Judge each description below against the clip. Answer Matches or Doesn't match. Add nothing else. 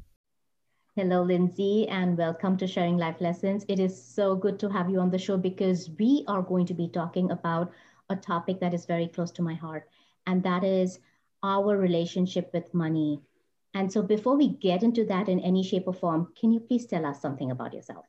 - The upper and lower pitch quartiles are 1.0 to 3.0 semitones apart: Matches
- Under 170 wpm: Doesn't match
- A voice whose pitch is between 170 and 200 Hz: Matches